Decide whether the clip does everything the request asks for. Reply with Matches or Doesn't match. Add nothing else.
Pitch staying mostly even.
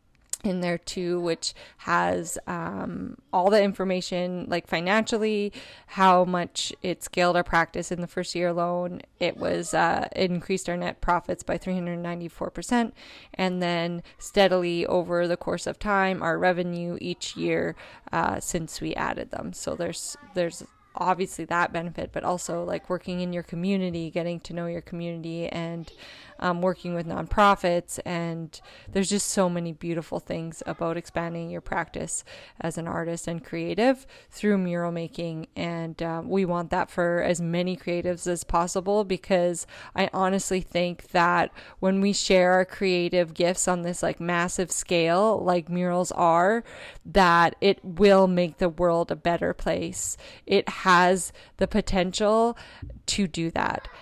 Matches